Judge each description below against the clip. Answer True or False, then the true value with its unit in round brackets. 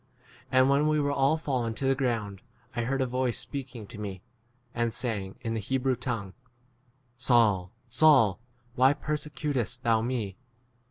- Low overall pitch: True (125 Hz)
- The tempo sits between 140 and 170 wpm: True (165 wpm)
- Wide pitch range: False (3.2 semitones)